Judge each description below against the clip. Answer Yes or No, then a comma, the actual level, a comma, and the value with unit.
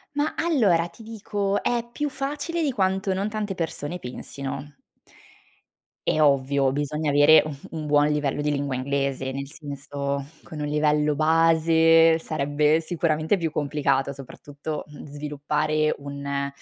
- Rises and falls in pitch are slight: No, average, 3.0 semitones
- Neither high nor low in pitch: Yes, medium, 150 Hz